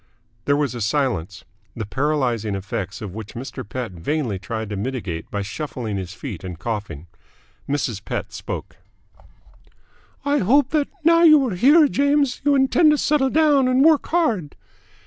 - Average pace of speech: Yes, average, 165 wpm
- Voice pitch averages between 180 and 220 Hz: No, low, 135 Hz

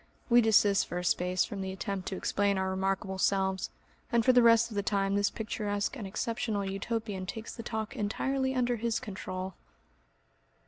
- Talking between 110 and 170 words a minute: No, average, 180 wpm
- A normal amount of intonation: Yes, average, 3.1 semitones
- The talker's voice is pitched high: Yes, high, 205 Hz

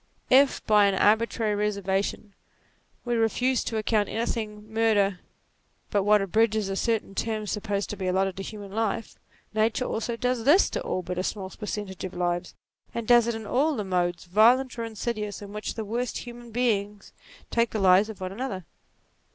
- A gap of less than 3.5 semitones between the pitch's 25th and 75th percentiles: Yes, average, 2.7 semitones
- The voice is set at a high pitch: Yes, high, 215 Hz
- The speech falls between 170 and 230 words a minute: Yes, average, 180 wpm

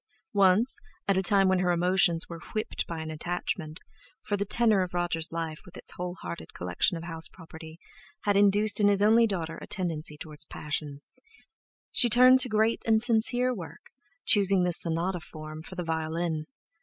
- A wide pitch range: No, average, 4.1 semitones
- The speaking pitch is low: No, medium, 180 Hz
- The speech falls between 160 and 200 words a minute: Yes, average, 170 wpm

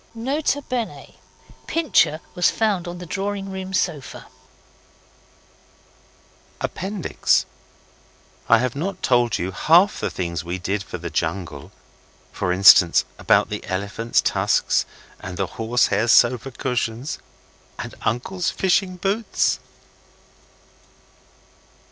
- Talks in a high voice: No, medium, 140 Hz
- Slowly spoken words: Yes, slow, 105 wpm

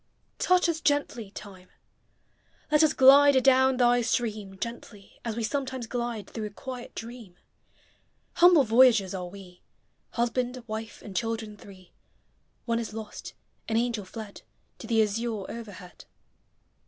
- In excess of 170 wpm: No, average, 145 wpm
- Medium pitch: No, high, 230 Hz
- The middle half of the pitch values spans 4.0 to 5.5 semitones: No, average, 3.4 semitones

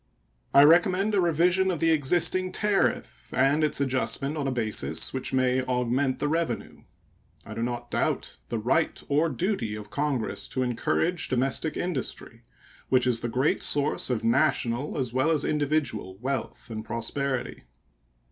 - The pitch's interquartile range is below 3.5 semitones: No, average, 4.4 semitones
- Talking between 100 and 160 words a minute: Yes, average, 155 wpm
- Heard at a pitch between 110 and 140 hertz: Yes, low, 135 Hz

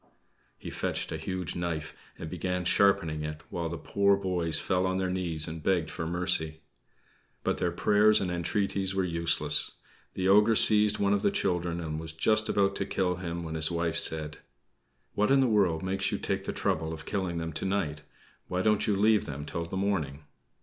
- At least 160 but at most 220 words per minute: Yes, average, 200 wpm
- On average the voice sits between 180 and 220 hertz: No, very low, 90 Hz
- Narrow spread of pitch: No, average, 3.2 semitones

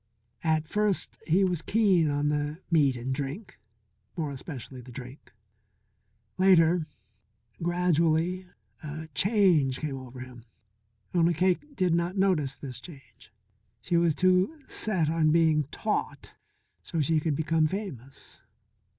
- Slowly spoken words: Yes, slow, 125 wpm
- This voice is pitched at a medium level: Yes, medium, 160 Hz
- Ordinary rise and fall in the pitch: Yes, average, 4.0 semitones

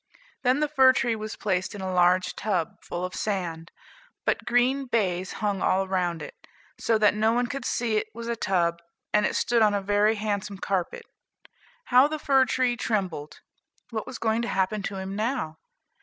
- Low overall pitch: No, high, 210 Hz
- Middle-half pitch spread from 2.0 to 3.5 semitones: No, average, 4.2 semitones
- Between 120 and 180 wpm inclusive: No, average, 190 wpm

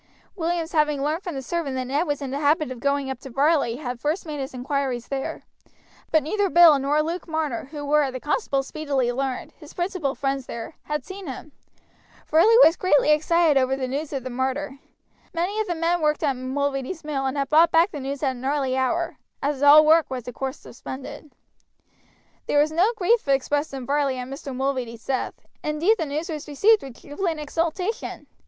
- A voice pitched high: Yes, very high, 290 Hz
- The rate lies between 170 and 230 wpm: Yes, average, 200 wpm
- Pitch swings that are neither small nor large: Yes, average, 3.2 semitones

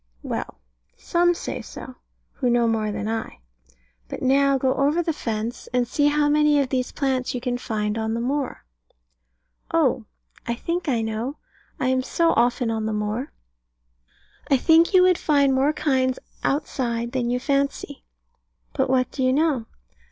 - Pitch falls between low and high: No, very high, 260 Hz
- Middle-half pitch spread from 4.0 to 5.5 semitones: No, average, 3.5 semitones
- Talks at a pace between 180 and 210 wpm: No, average, 165 wpm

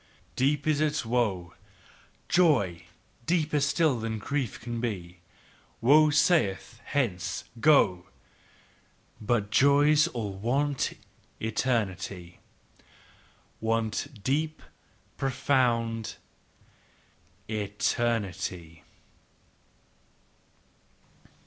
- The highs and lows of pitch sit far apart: Yes, wide, 5.9 semitones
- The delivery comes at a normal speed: No, slow, 70 wpm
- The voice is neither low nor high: No, low, 120 Hz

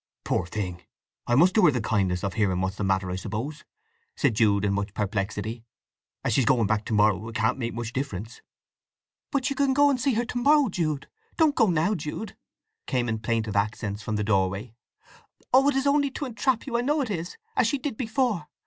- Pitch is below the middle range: Yes, low, 120 Hz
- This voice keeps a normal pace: No, fast, 215 wpm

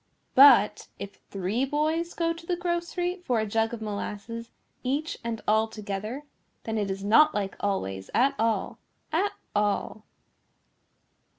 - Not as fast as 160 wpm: Yes, average, 140 wpm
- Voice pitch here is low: No, high, 230 Hz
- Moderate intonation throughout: No, wide, 6.8 semitones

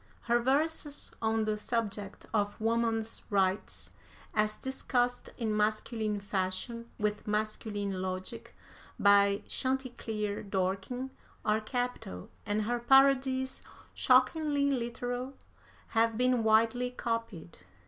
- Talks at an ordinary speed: No, slow, 100 wpm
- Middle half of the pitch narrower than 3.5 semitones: Yes, average, 3.1 semitones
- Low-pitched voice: No, high, 225 Hz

